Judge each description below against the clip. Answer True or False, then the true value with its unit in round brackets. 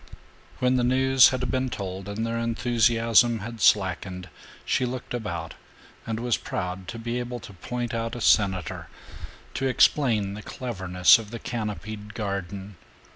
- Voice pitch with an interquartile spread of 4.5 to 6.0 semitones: False (3.7 semitones)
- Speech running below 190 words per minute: True (150 wpm)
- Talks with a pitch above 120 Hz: False (115 Hz)